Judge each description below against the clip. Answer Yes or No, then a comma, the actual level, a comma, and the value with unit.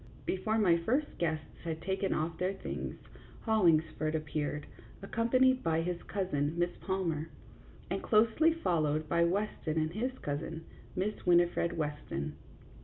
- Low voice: No, medium, 170 Hz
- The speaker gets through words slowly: Yes, slow, 130 wpm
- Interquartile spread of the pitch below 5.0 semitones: Yes, average, 4.5 semitones